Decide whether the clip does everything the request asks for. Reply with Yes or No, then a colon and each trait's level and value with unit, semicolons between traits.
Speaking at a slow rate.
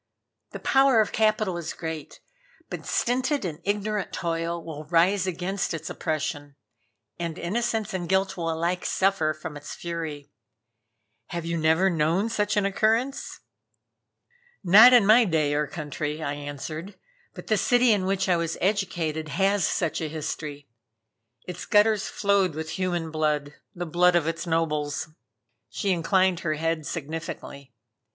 No: average, 145 wpm